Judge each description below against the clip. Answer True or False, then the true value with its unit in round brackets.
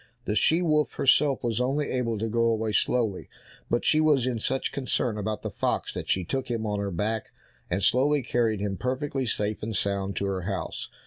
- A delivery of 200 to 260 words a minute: True (205 wpm)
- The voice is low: True (115 Hz)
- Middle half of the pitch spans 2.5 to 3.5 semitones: False (4.1 semitones)